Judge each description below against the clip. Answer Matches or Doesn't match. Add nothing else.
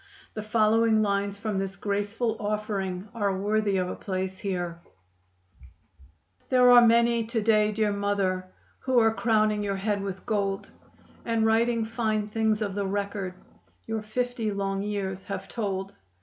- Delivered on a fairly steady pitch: Matches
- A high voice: Matches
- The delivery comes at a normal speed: Matches